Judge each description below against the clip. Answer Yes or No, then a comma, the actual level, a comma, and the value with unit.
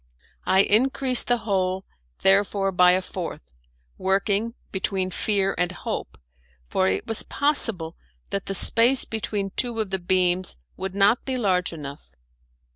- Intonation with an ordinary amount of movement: Yes, average, 3.4 semitones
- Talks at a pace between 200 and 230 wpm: No, average, 140 wpm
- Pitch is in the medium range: No, high, 195 Hz